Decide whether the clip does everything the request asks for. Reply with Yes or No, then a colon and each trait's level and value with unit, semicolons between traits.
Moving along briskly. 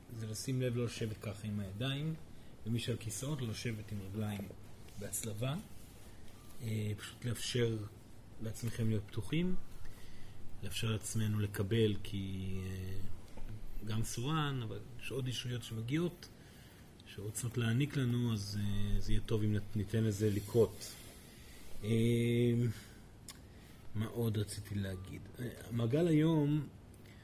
No: average, 105 wpm